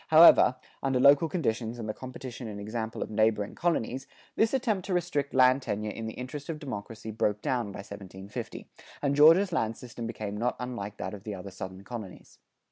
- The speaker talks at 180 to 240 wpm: Yes, average, 190 wpm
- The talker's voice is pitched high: No, low, 120 Hz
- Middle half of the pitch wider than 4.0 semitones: Yes, average, 5.1 semitones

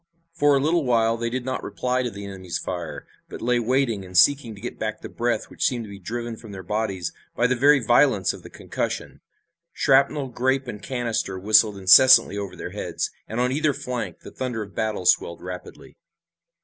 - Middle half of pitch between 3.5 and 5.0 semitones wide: Yes, average, 4.1 semitones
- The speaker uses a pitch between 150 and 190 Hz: No, low, 115 Hz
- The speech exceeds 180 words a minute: Yes, fast, 205 wpm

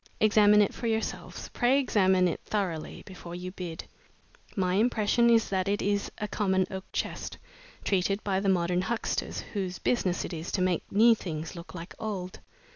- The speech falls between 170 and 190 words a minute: Yes, average, 175 wpm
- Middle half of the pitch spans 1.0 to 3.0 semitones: Yes, average, 2.7 semitones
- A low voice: No, high, 190 Hz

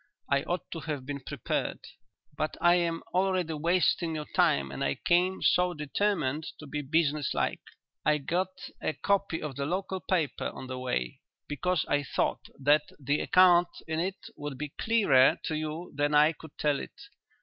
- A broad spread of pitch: No, average, 3.7 semitones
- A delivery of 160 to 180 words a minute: Yes, average, 175 wpm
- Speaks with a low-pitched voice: No, medium, 155 Hz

